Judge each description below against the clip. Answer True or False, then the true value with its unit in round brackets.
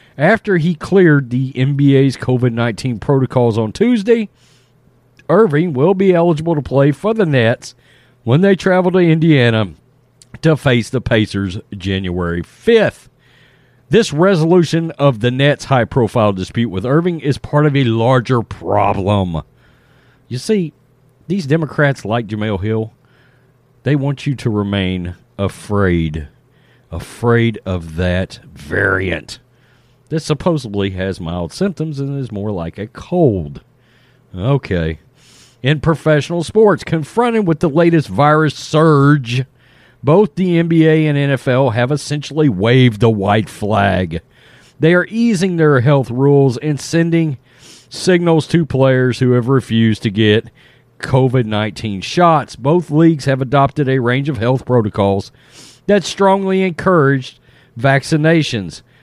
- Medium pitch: False (130 Hz)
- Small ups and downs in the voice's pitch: False (5.1 semitones)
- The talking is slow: True (130 wpm)